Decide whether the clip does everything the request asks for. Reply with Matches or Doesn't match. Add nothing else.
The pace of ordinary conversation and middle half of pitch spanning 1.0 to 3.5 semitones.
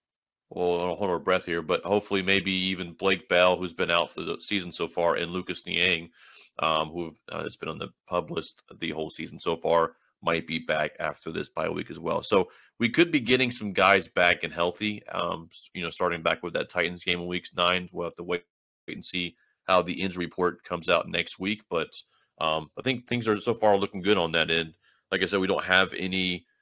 Doesn't match